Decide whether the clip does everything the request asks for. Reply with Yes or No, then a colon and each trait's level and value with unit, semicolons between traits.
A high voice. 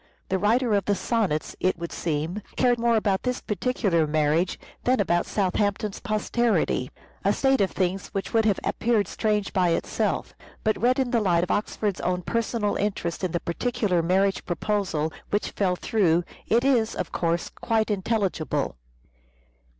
Yes: high, 200 Hz